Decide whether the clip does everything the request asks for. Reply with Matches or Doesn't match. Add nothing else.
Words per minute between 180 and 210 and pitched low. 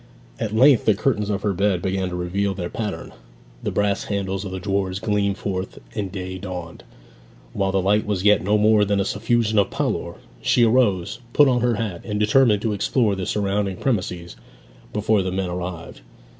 Matches